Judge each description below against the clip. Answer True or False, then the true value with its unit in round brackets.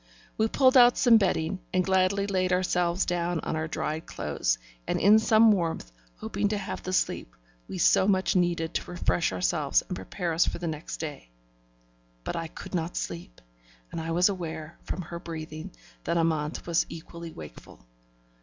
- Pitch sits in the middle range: True (170 Hz)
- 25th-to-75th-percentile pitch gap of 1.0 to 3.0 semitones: True (2.6 semitones)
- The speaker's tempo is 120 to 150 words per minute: False (175 wpm)